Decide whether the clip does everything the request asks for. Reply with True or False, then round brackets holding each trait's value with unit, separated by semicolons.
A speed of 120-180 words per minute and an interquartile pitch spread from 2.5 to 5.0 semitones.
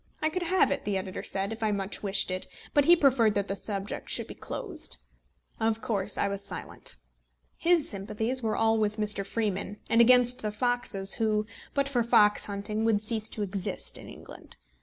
False (195 wpm; 3.4 semitones)